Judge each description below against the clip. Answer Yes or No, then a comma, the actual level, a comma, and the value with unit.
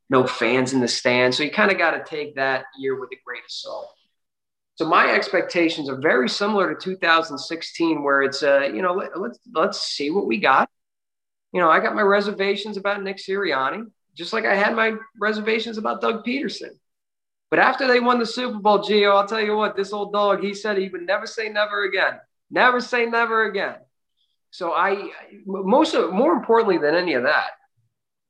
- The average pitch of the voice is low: No, high, 200 Hz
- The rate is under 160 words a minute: No, average, 200 wpm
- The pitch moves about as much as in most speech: No, wide, 7.4 semitones